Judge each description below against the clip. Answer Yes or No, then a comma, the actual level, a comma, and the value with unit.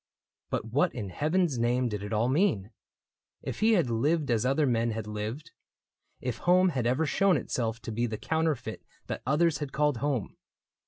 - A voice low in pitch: Yes, low, 130 Hz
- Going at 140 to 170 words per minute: No, average, 180 wpm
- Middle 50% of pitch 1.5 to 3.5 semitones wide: No, wide, 5.5 semitones